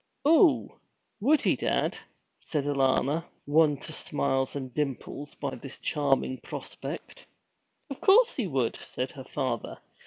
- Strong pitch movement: No, average, 3.6 semitones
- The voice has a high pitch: No, medium, 145 Hz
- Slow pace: Yes, slow, 130 wpm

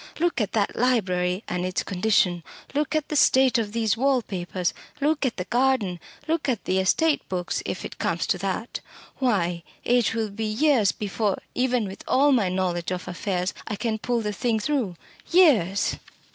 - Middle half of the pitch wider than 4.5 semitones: Yes, wide, 5.6 semitones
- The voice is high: Yes, high, 220 Hz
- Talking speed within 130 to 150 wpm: No, average, 180 wpm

